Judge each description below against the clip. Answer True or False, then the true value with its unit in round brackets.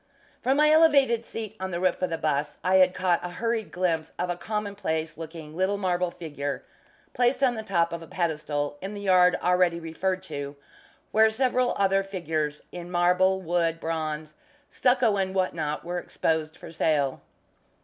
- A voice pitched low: False (180 Hz)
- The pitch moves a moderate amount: True (3.6 semitones)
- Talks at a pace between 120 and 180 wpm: True (175 wpm)